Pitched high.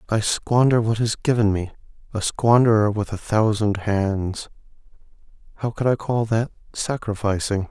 No: low, 110 Hz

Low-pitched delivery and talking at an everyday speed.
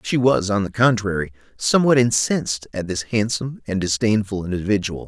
Yes: low, 110 Hz; average, 155 wpm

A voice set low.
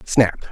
Yes: low, 110 Hz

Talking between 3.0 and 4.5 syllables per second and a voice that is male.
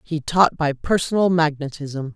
No: 4.4 syllables/s; female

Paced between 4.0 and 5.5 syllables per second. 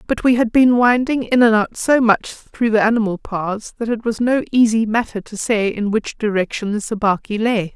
Yes: 5.0 syllables/s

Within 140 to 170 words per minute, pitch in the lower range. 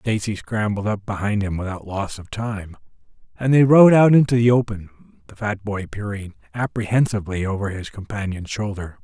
Yes: average, 165 wpm; low, 105 Hz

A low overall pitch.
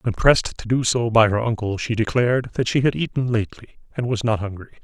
Yes: low, 115 Hz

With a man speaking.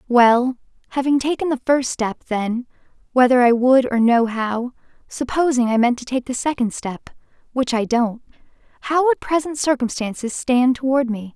No: female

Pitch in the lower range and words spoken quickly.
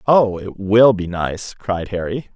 No: low, 100 Hz; average, 180 wpm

